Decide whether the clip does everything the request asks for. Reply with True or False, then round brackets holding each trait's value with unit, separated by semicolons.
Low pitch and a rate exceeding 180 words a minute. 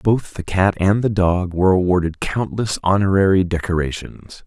False (95 Hz; 150 wpm)